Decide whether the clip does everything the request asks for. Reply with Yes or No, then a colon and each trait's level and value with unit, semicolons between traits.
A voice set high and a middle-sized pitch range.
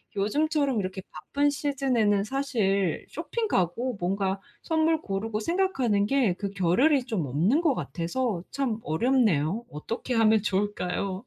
No: high, 220 Hz; wide, 6.0 semitones